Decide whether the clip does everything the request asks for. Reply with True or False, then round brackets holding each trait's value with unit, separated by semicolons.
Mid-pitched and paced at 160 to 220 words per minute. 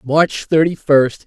False (150 Hz; 140 wpm)